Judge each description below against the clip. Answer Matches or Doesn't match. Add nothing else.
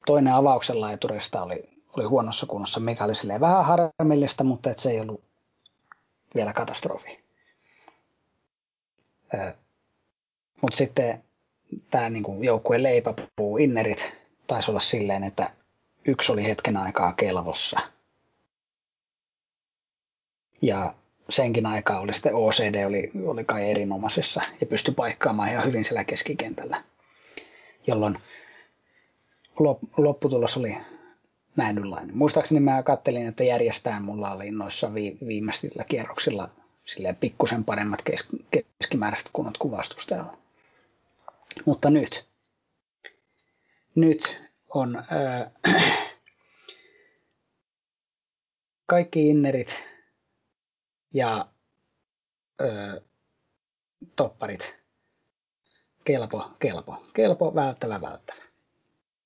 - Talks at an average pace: Doesn't match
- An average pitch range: Doesn't match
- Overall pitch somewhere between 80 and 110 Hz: Doesn't match